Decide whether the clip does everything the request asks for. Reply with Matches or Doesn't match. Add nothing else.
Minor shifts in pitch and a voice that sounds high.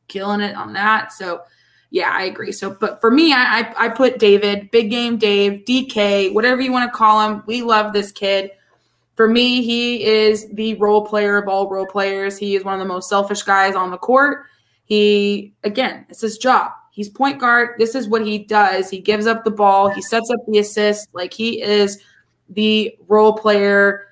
Matches